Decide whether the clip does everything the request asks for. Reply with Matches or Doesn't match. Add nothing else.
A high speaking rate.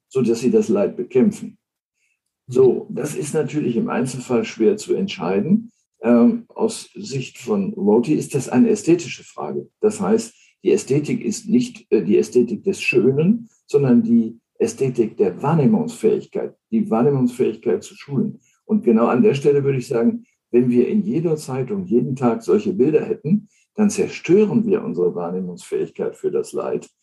Doesn't match